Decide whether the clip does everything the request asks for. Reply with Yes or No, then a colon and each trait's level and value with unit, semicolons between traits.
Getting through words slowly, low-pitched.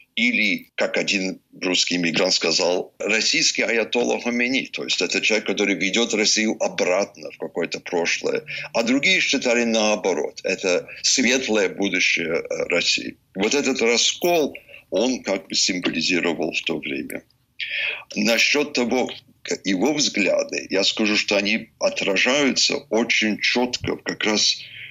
No: average, 125 wpm; low, 120 Hz